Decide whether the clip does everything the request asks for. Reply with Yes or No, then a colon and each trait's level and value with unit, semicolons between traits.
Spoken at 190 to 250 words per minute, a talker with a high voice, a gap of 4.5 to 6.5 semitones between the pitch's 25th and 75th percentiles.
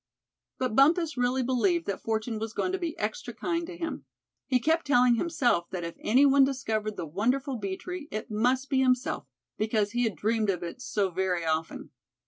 Yes: average, 195 wpm; high, 245 Hz; average, 4.8 semitones